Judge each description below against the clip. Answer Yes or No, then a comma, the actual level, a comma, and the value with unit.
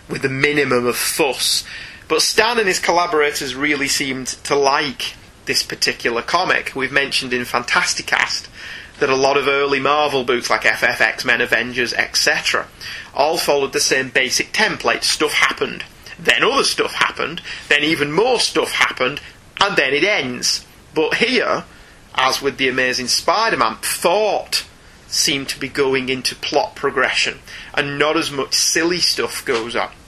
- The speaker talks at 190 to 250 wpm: No, average, 155 wpm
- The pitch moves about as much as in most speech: No, narrow, 2.1 semitones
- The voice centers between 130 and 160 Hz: Yes, medium, 140 Hz